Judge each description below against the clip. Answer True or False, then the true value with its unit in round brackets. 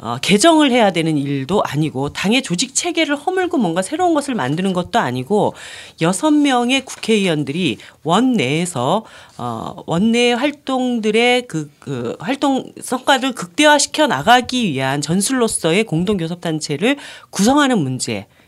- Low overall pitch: False (225 Hz)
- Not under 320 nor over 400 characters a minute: False (300 characters per minute)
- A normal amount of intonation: False (8.7 semitones)